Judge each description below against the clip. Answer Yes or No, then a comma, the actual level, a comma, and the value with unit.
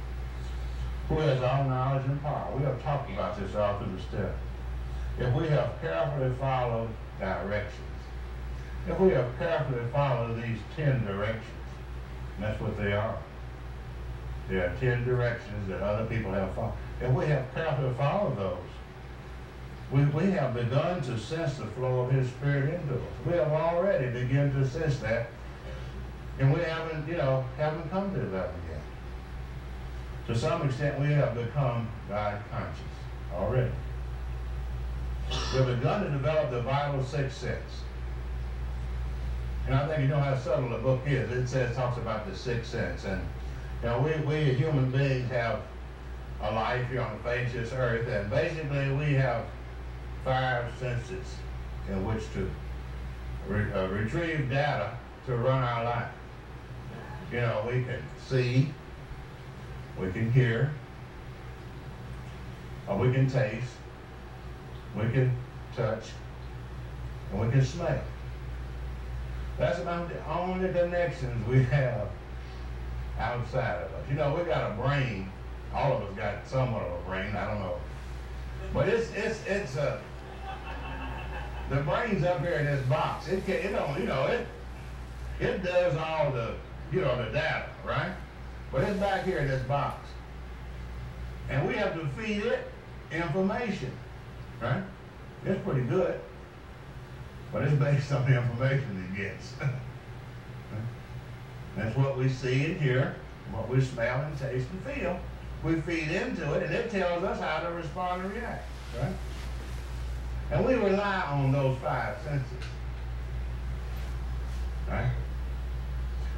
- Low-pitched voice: Yes, low, 115 Hz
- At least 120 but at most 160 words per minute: Yes, average, 145 wpm